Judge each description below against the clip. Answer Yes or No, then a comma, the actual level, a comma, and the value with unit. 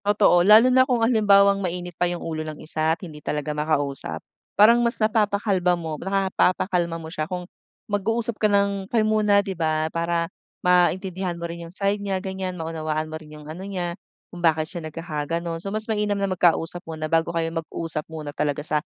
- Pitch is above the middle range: No, medium, 175 Hz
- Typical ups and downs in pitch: Yes, average, 3.8 semitones